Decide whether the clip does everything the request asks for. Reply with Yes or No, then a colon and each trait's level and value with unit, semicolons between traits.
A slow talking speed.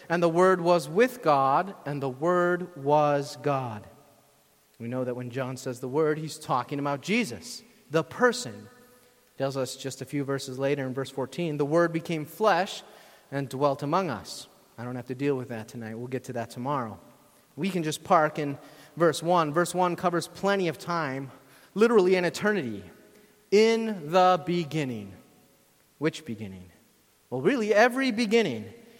No: average, 170 wpm